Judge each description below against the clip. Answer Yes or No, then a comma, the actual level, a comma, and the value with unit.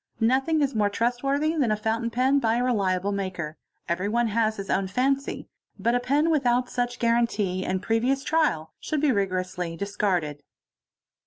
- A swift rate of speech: No, average, 155 wpm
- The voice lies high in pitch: Yes, high, 230 Hz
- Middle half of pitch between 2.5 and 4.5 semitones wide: No, average, 5.0 semitones